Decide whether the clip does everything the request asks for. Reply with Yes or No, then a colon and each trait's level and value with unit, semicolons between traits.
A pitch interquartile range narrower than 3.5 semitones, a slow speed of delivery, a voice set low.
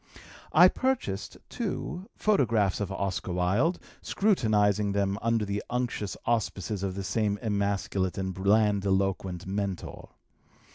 Yes: average, 2.9 semitones; slow, 110 wpm; low, 100 Hz